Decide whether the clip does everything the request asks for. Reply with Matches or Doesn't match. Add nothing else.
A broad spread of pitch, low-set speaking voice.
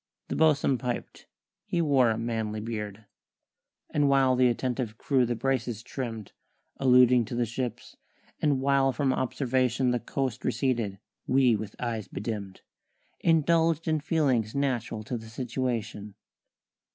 Doesn't match